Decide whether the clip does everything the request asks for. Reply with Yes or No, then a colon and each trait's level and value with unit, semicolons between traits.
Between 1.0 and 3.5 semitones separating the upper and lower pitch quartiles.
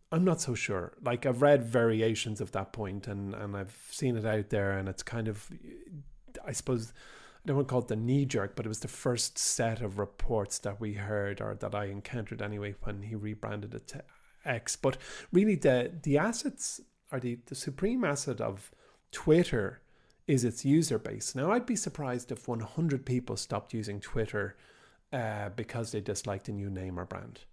No: average, 4.9 semitones